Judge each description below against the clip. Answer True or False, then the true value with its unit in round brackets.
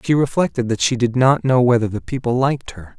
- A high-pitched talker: False (125 Hz)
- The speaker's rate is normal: False (240 wpm)